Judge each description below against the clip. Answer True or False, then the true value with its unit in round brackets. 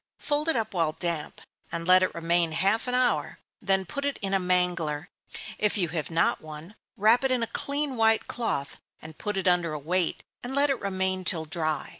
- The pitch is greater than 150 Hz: True (185 Hz)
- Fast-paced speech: True (210 wpm)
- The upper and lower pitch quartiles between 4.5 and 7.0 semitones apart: True (5.2 semitones)